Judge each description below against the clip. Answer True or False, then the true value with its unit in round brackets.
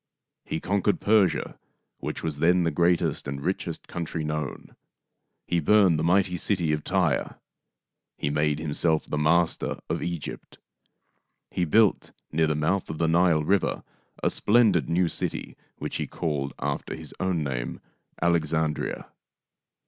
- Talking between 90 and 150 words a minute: True (145 wpm)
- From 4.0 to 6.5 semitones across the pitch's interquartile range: False (2.9 semitones)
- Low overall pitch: True (80 Hz)